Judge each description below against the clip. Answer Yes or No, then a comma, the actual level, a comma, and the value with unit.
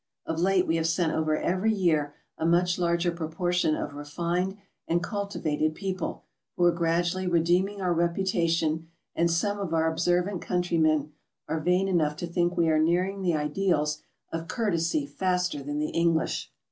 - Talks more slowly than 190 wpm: Yes, average, 165 wpm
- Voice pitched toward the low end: No, medium, 170 Hz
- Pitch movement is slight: Yes, narrow, 2.1 semitones